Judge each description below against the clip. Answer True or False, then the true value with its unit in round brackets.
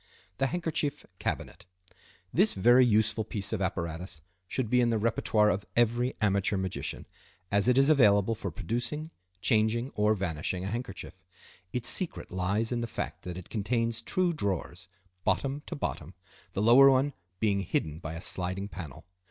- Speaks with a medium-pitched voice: False (110 Hz)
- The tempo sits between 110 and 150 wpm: False (160 wpm)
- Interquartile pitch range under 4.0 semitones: False (4.6 semitones)